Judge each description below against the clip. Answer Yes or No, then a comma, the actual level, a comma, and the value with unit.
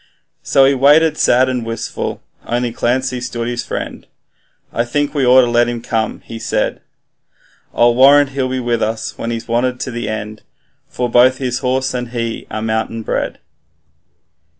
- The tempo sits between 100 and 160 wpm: No, average, 175 wpm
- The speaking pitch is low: Yes, low, 120 Hz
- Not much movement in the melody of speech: Yes, narrow, 2.0 semitones